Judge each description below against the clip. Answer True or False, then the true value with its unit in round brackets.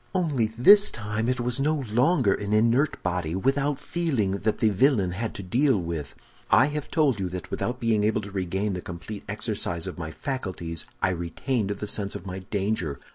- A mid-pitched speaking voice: False (105 Hz)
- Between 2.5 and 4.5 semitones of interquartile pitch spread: False (5.6 semitones)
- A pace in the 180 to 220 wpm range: True (190 wpm)